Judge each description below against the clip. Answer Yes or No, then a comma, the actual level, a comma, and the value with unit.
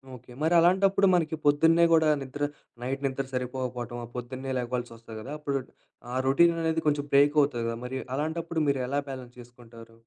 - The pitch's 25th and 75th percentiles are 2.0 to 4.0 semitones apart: No, average, 4.4 semitones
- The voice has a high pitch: No, low, 135 Hz